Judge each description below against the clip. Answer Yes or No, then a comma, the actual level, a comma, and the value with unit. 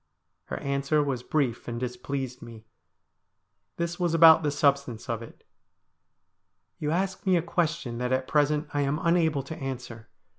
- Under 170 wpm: Yes, average, 160 wpm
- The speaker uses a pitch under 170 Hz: Yes, medium, 140 Hz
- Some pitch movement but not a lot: Yes, average, 4.3 semitones